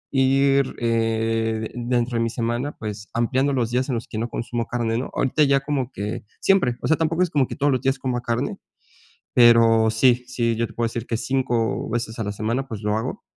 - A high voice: No, low, 120 Hz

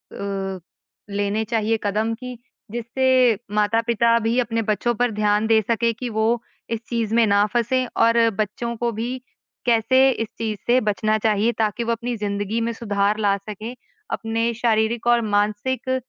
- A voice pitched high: Yes, high, 225 Hz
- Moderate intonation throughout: No, narrow, 2.0 semitones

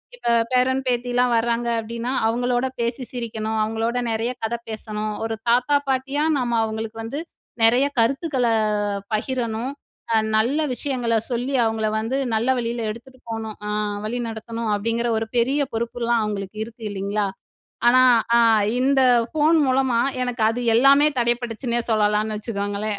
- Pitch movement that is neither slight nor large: No, narrow, 2.1 semitones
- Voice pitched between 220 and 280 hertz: Yes, high, 235 Hz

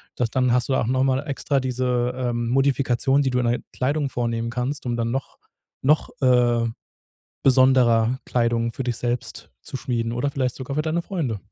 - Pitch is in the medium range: No, low, 125 Hz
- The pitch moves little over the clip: Yes, narrow, 2.0 semitones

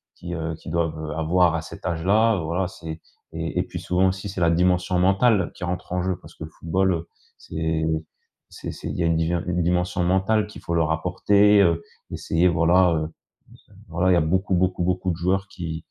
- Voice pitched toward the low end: Yes, very low, 90 Hz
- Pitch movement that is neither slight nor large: No, narrow, 2.1 semitones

